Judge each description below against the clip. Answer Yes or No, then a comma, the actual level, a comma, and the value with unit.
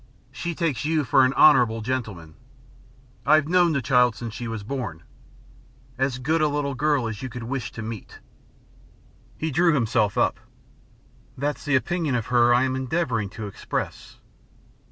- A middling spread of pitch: Yes, average, 4.5 semitones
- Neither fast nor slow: Yes, average, 160 wpm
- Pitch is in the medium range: No, low, 130 Hz